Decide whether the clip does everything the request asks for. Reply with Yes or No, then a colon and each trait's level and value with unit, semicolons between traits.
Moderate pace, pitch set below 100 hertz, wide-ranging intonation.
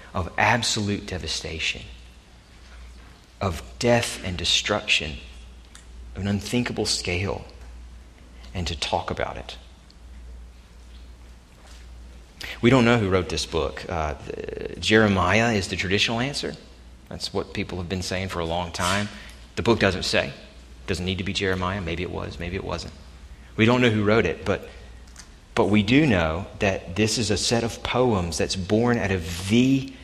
Yes: average, 160 wpm; very low, 90 Hz; wide, 8.4 semitones